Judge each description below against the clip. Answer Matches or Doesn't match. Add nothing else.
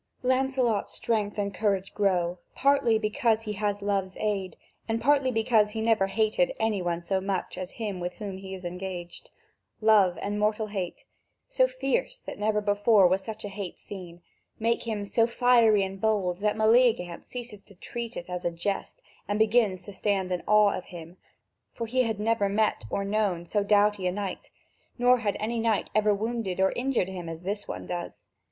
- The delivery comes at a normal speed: Matches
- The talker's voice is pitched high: Matches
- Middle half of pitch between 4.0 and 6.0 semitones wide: Doesn't match